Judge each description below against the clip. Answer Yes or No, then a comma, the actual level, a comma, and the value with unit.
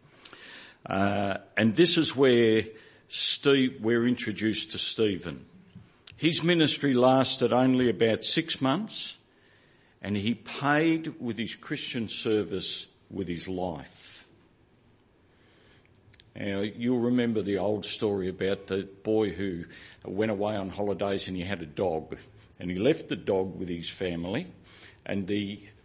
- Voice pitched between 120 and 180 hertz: No, low, 105 Hz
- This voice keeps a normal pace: No, slow, 130 wpm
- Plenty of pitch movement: No, average, 3.8 semitones